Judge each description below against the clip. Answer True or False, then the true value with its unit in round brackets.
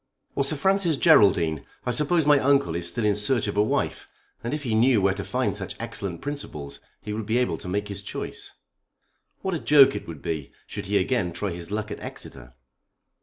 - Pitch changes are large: True (7.3 semitones)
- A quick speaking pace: True (215 wpm)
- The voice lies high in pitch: False (105 Hz)